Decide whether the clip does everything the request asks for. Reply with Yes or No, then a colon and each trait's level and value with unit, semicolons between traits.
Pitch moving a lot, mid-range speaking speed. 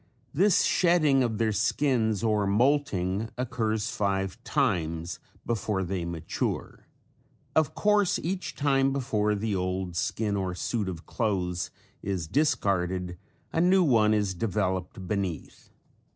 No: wide, 5.7 semitones; slow, 125 wpm